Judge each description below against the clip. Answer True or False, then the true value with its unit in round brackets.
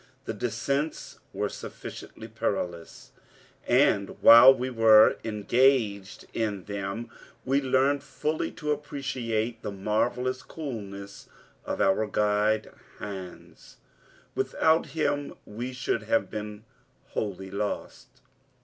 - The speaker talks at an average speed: False (105 wpm)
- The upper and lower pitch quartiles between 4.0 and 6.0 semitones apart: True (4.3 semitones)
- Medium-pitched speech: False (110 Hz)